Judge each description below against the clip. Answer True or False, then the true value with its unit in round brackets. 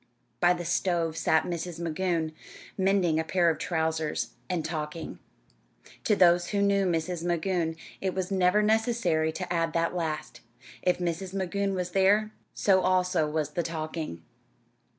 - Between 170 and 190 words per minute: False (150 wpm)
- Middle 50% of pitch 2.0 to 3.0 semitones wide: True (2.7 semitones)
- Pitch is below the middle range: False (175 Hz)